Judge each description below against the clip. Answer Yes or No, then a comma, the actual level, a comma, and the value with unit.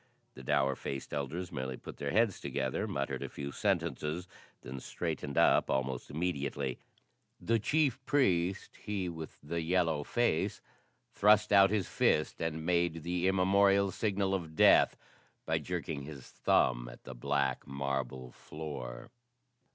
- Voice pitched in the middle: No, very low, 80 Hz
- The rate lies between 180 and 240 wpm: No, average, 140 wpm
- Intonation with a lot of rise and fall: Yes, wide, 5.8 semitones